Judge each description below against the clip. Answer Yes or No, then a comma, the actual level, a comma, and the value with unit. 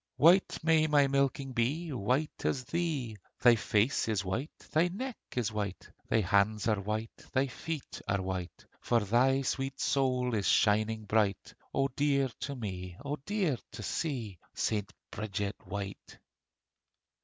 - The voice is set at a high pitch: No, low, 120 Hz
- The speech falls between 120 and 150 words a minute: Yes, average, 145 wpm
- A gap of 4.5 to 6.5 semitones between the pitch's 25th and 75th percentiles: Yes, average, 5.2 semitones